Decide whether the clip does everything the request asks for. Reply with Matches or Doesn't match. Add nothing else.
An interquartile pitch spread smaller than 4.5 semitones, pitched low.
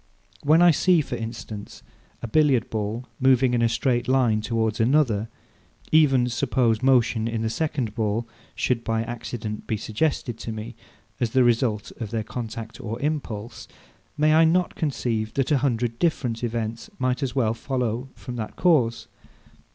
Matches